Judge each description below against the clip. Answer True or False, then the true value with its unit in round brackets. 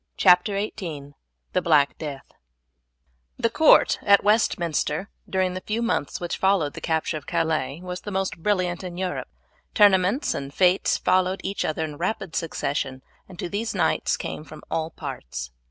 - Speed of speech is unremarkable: True (160 wpm)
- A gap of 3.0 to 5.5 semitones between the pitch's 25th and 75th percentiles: True (3.9 semitones)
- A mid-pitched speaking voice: True (180 Hz)